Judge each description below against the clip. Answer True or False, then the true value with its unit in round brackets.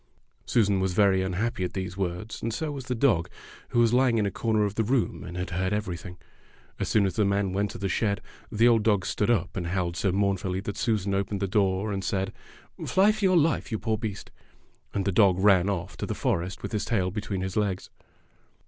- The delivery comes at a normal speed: False (230 wpm)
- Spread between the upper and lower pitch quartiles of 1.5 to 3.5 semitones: True (2.7 semitones)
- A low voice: True (100 Hz)